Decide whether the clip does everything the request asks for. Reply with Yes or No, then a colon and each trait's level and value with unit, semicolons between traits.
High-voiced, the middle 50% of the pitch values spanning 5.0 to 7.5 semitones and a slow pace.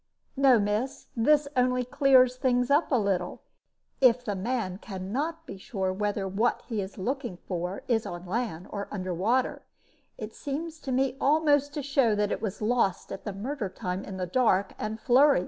No: high, 230 Hz; wide, 5.4 semitones; average, 185 wpm